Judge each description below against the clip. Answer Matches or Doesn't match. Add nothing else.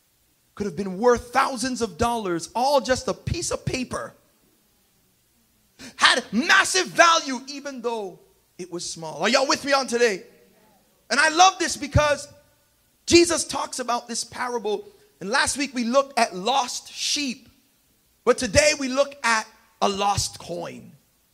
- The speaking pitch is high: Matches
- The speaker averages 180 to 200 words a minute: Doesn't match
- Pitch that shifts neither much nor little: Matches